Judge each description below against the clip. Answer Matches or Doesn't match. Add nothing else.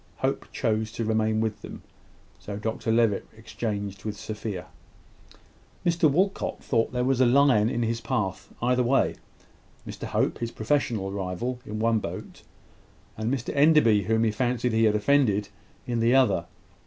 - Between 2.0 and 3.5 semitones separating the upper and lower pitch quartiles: Matches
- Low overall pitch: Matches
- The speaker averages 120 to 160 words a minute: Matches